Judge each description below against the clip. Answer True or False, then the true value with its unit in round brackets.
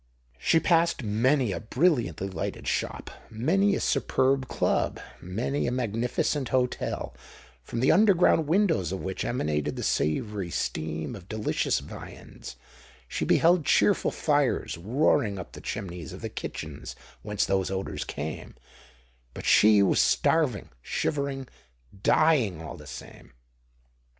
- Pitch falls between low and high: False (110 Hz)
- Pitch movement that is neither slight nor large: False (8.3 semitones)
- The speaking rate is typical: False (120 wpm)